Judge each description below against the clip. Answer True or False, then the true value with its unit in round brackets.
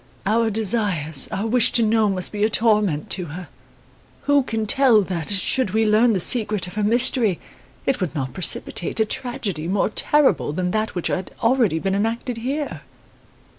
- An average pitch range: True (4.0 semitones)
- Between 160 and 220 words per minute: True (175 wpm)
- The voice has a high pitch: True (215 Hz)